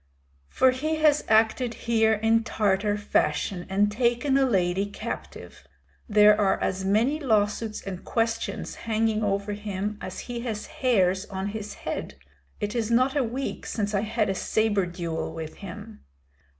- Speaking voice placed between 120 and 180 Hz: No, high, 215 Hz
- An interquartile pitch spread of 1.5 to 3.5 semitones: Yes, average, 2.8 semitones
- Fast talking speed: No, average, 155 wpm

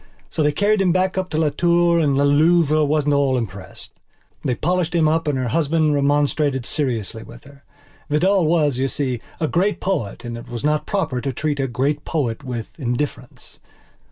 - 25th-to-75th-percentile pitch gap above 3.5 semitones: Yes, average, 3.9 semitones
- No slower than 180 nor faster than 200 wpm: Yes, average, 190 wpm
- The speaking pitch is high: No, medium, 145 Hz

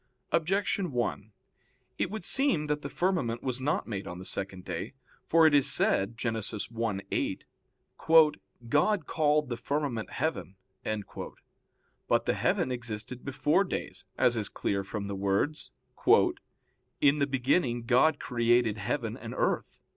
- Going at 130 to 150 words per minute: Yes, average, 140 wpm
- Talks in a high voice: No, low, 125 Hz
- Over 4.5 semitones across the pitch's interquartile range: Yes, wide, 5.4 semitones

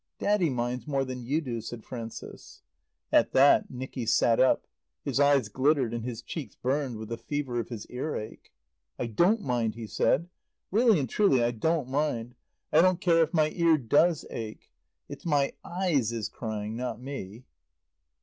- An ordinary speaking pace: Yes, average, 170 wpm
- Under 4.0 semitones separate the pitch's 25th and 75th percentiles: No, average, 4.7 semitones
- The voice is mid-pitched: No, low, 130 Hz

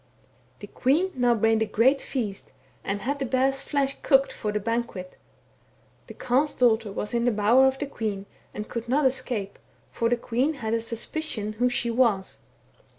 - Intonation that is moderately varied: Yes, average, 3.4 semitones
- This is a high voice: Yes, high, 240 Hz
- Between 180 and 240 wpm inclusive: Yes, average, 185 wpm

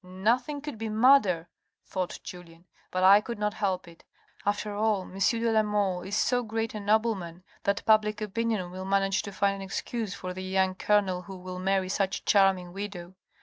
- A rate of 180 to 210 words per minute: Yes, average, 200 wpm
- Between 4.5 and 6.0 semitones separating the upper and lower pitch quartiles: No, narrow, 2.6 semitones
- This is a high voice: Yes, high, 195 Hz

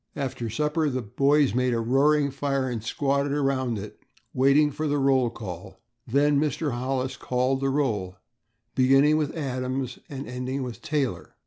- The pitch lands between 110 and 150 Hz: Yes, low, 135 Hz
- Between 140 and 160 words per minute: Yes, average, 155 wpm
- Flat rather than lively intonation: Yes, narrow, 2.3 semitones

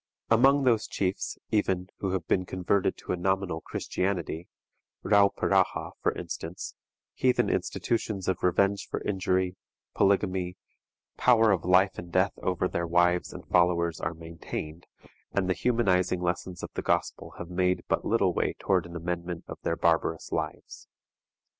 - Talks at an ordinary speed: Yes, average, 145 wpm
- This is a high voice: No, very low, 90 Hz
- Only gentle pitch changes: Yes, narrow, 2.1 semitones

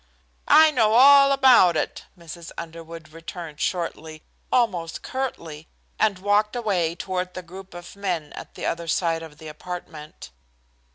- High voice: No, medium, 175 Hz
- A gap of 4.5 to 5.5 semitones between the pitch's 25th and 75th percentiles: No, average, 4.1 semitones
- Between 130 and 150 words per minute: Yes, average, 145 wpm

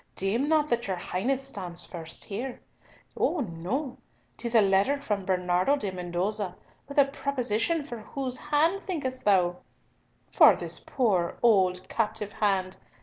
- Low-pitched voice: No, high, 215 Hz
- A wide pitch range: Yes, wide, 6.5 semitones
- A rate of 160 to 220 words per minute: No, average, 145 wpm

